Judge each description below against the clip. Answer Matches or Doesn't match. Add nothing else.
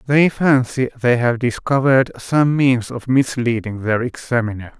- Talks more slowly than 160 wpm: Matches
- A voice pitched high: Doesn't match